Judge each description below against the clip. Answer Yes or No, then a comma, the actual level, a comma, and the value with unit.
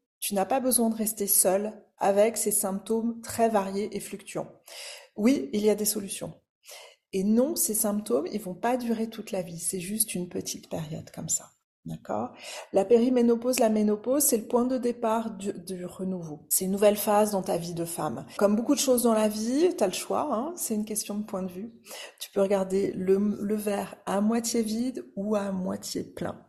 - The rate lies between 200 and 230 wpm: Yes, average, 210 wpm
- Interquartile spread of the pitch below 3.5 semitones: Yes, average, 2.7 semitones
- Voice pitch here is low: No, high, 210 Hz